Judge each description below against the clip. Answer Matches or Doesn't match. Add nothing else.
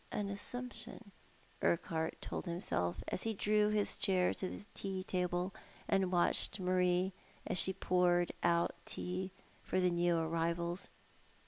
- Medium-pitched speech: Matches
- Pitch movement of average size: Doesn't match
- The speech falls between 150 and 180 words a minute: Doesn't match